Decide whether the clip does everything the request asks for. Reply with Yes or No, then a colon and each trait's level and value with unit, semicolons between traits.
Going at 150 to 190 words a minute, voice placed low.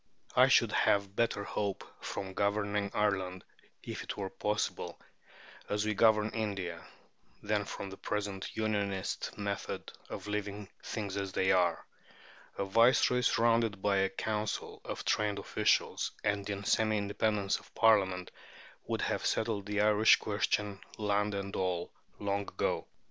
No: average, 140 wpm; low, 100 Hz